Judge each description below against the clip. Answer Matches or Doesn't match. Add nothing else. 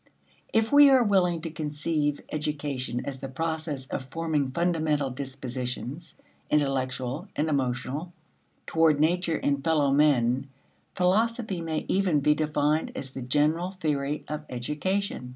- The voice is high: Doesn't match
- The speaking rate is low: Matches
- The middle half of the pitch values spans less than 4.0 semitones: Matches